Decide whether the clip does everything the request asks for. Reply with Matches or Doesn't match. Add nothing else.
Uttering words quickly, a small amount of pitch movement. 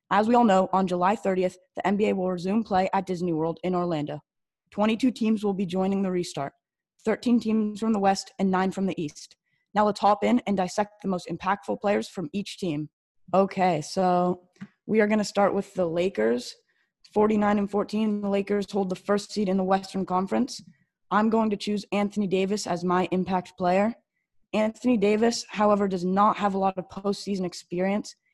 Doesn't match